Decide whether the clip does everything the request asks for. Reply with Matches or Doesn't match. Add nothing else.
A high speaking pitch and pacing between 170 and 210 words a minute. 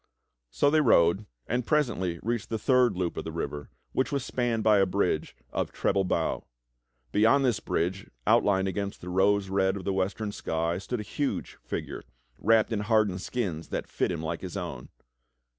Doesn't match